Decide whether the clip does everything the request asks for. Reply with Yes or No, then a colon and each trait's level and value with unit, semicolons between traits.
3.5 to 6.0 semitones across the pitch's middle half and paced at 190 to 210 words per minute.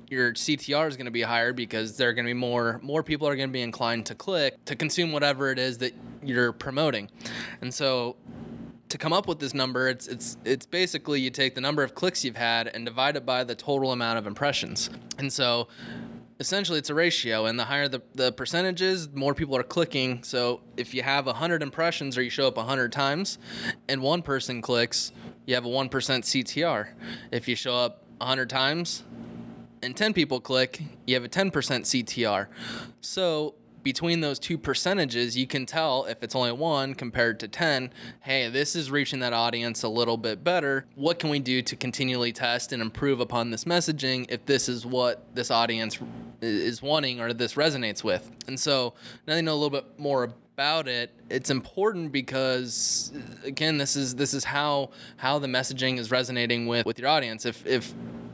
No: average, 3.0 semitones; average, 195 wpm